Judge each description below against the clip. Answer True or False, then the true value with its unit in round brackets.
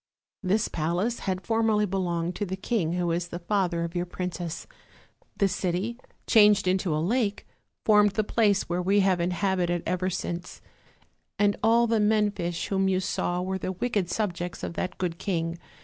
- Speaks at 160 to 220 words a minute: True (175 wpm)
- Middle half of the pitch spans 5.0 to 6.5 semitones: False (2.9 semitones)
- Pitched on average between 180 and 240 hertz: True (185 Hz)